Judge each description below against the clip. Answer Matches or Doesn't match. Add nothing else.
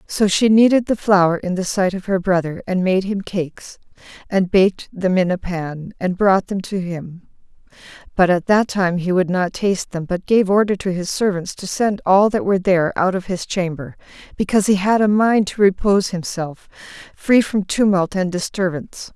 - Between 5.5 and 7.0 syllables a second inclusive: Doesn't match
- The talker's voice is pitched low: Doesn't match